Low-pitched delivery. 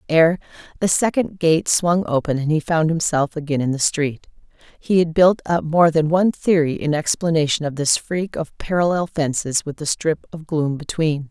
No: medium, 160 Hz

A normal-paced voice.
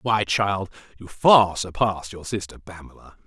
Yes: average, 145 wpm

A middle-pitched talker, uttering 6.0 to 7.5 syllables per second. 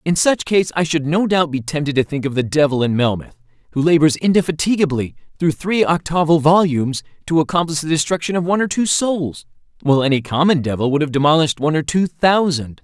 Yes: medium, 155 Hz; 6.1 syllables/s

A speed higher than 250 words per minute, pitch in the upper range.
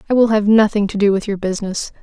Yes: fast, 265 wpm; high, 205 Hz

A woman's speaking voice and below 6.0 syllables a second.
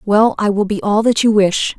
Yes: female; 5.0 syllables/s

